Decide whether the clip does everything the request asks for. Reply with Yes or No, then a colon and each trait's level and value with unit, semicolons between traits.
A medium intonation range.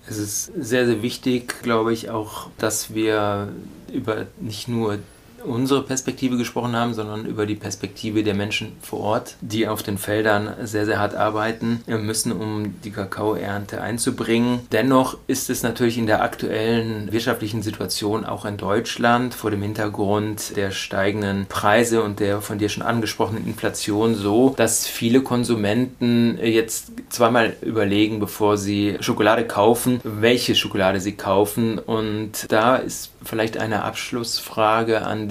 No: narrow, 2.0 semitones